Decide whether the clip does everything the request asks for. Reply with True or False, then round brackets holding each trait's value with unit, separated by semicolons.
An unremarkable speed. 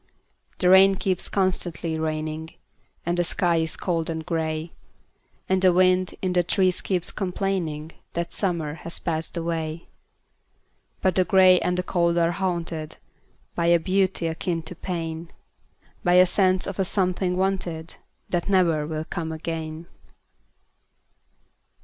False (120 wpm)